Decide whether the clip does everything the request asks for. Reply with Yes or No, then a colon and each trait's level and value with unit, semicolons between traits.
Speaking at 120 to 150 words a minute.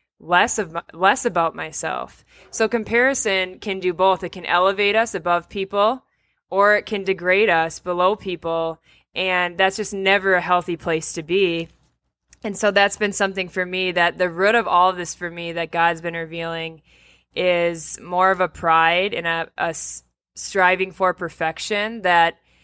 No: average, 170 wpm